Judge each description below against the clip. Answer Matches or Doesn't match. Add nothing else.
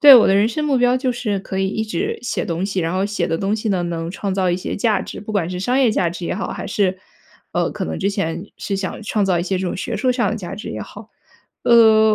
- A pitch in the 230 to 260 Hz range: Doesn't match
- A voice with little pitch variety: Doesn't match